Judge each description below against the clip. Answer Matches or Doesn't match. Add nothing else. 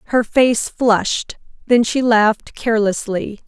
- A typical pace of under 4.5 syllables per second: Matches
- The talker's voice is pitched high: Matches